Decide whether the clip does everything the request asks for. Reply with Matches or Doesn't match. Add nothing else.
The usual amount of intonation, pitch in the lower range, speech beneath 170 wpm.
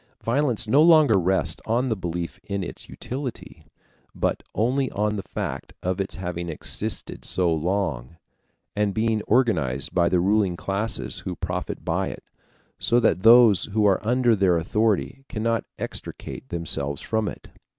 Matches